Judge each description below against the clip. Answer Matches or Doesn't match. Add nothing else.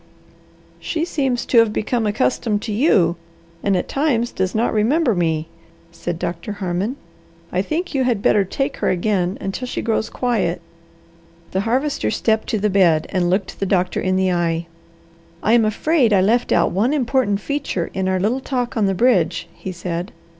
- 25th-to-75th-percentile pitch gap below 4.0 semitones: Doesn't match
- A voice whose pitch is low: Doesn't match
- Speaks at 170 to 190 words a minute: Matches